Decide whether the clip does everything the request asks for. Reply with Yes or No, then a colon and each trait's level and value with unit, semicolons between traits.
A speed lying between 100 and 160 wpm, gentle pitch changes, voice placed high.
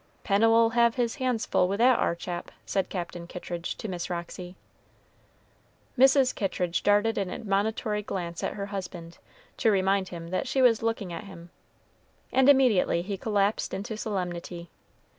No: average, 155 wpm; average, 4.2 semitones; high, 200 Hz